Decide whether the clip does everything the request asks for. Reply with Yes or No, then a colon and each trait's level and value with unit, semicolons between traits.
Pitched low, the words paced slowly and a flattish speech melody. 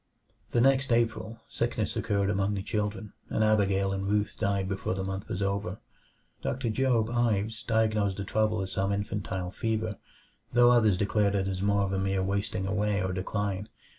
No: low, 100 Hz; average, 175 wpm; narrow, 2.1 semitones